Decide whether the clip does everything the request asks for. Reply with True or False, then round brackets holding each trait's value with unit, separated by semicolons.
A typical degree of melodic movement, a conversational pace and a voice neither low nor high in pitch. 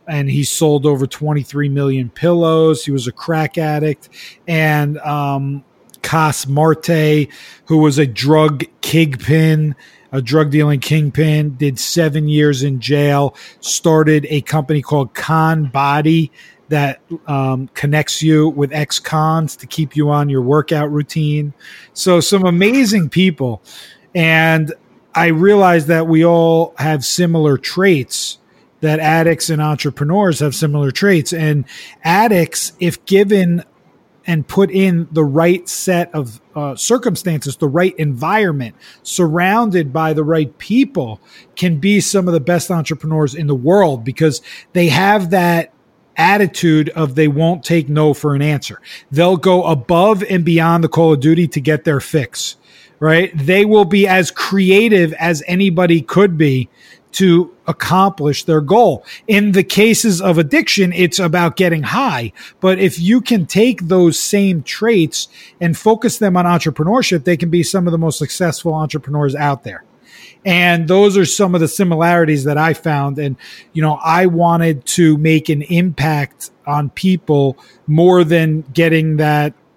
True (3.1 semitones; 150 wpm; 160 Hz)